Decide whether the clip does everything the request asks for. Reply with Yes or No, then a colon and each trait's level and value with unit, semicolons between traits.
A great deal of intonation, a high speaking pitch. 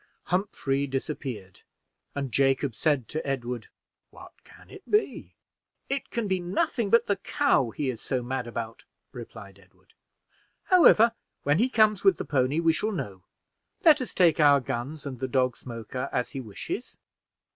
No: wide, 7.9 semitones; medium, 140 Hz